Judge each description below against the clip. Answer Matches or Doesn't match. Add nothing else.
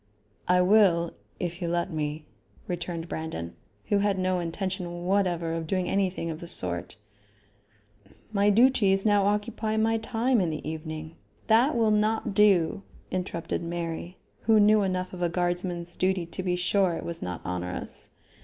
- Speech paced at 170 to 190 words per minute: Doesn't match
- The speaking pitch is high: Doesn't match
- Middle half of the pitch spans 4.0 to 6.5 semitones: Doesn't match